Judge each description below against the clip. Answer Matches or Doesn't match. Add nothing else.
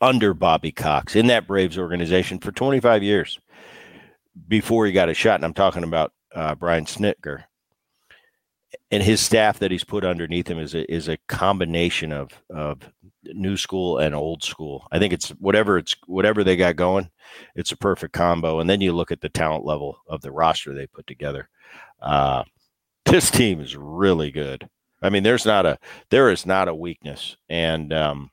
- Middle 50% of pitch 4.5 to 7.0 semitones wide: Doesn't match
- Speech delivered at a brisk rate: Doesn't match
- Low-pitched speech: Matches